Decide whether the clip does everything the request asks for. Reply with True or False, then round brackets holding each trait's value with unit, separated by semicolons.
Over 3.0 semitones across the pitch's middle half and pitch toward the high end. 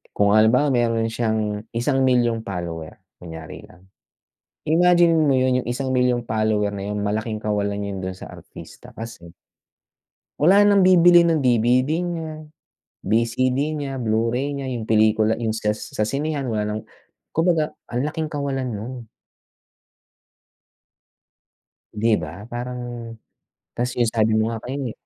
False (4.3 semitones; 120 Hz)